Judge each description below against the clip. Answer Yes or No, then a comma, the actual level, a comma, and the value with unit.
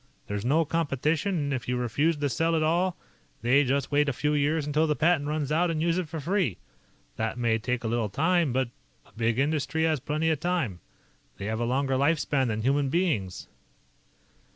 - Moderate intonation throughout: Yes, average, 4.5 semitones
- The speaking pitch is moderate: Yes, medium, 145 Hz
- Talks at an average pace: No, fast, 210 wpm